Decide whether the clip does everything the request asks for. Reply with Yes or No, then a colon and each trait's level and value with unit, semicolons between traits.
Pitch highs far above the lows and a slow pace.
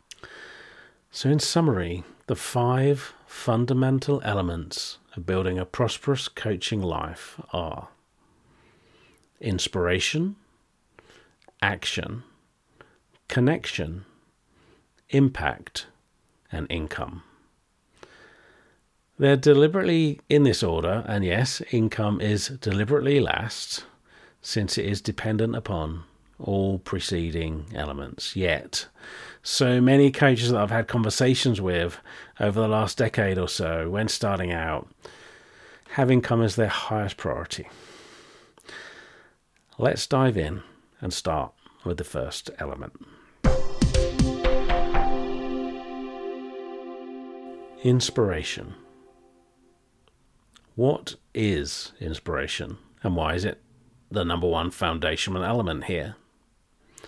Yes: wide, 6.7 semitones; slow, 90 wpm